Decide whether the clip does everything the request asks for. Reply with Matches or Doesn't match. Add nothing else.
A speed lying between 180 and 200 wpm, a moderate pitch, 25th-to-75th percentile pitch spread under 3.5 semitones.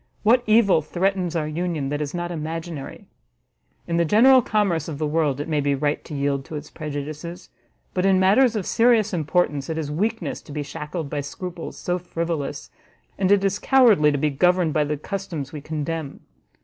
Doesn't match